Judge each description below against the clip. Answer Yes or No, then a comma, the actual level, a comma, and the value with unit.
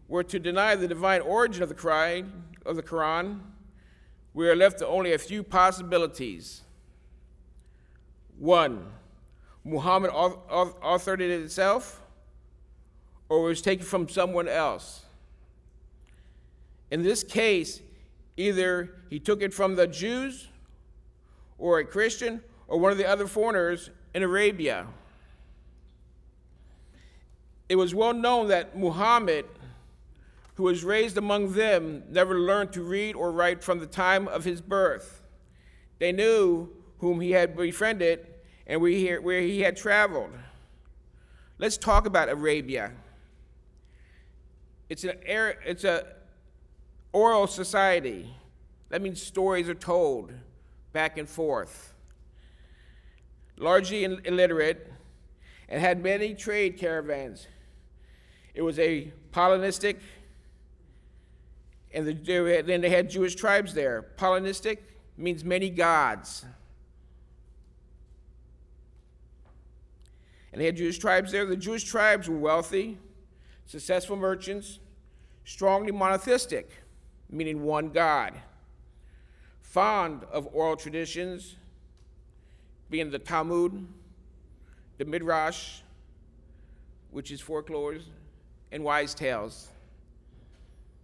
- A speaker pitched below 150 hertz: No, medium, 160 Hz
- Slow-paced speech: Yes, slow, 105 wpm